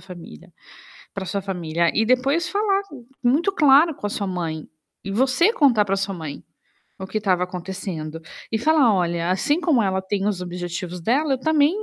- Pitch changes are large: Yes, wide, 7.2 semitones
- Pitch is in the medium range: No, high, 200 Hz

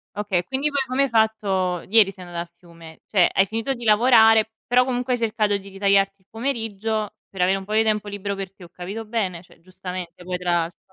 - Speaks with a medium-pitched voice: No, high, 200 Hz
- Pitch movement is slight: No, average, 3.3 semitones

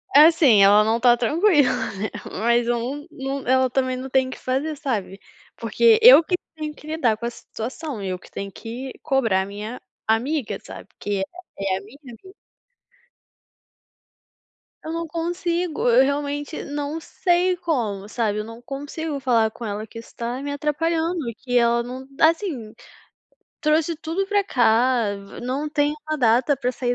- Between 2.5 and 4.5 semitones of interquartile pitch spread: No, average, 5.1 semitones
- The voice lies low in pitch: No, very high, 260 Hz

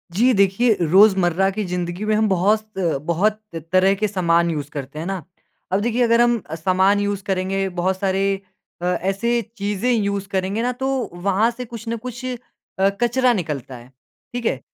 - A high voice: Yes, high, 195 Hz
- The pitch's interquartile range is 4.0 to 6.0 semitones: No, average, 3.4 semitones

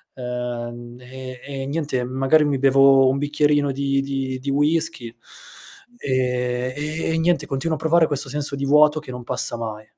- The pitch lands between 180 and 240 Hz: No, low, 135 Hz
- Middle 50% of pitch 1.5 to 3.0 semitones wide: Yes, average, 2.7 semitones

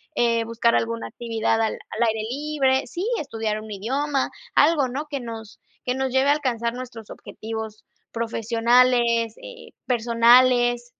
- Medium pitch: No, high, 235 Hz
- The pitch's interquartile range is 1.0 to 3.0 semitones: Yes, narrow, 2.5 semitones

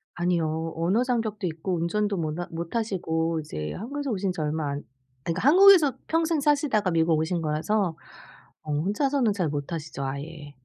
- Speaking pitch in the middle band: Yes, medium, 175 Hz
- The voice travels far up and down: Yes, wide, 5.7 semitones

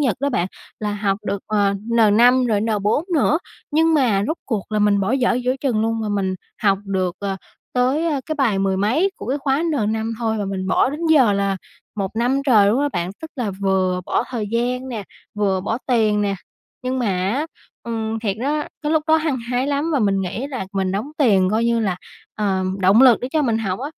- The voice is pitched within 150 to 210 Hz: No, high, 225 Hz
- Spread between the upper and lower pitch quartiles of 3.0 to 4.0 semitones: No, average, 4.8 semitones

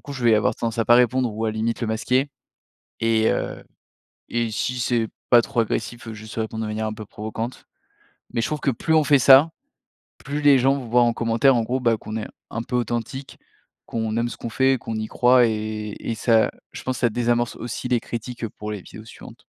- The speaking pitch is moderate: No, low, 115 Hz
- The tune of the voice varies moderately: No, narrow, 2.2 semitones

